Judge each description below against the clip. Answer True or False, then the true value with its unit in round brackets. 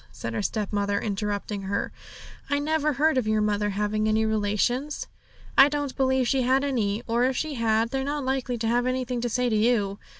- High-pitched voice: True (235 Hz)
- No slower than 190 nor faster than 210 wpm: True (200 wpm)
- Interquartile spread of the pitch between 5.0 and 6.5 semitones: False (4.1 semitones)